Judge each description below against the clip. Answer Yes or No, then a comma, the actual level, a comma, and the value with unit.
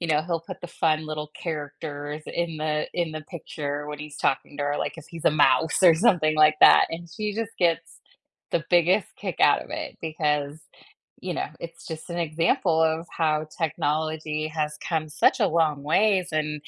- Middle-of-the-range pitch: Yes, medium, 155 Hz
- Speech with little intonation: Yes, narrow, 1.8 semitones